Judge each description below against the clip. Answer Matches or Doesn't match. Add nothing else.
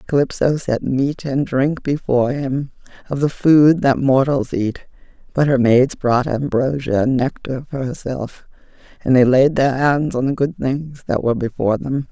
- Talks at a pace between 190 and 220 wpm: Doesn't match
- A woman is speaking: Matches